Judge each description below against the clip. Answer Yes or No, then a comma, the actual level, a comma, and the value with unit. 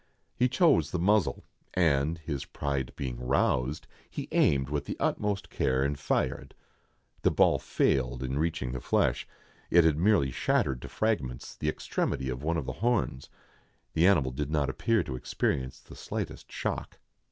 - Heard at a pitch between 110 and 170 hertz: No, very low, 70 Hz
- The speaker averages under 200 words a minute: Yes, average, 165 wpm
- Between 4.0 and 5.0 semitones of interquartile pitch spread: Yes, average, 4.6 semitones